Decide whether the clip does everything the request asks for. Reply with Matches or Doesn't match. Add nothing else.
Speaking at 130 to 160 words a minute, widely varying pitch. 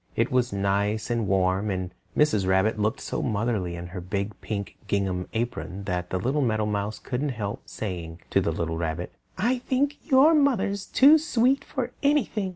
Doesn't match